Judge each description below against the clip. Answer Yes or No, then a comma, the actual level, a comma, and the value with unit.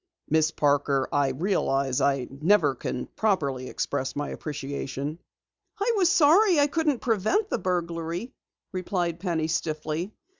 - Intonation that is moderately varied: No, wide, 7.2 semitones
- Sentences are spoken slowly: Yes, slow, 125 wpm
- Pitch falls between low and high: Yes, medium, 165 Hz